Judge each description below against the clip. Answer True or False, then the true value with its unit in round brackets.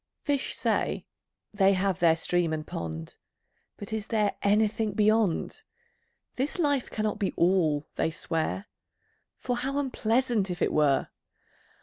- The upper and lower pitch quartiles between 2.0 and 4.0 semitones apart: False (5.0 semitones)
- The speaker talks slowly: True (130 wpm)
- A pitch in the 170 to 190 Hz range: False (205 Hz)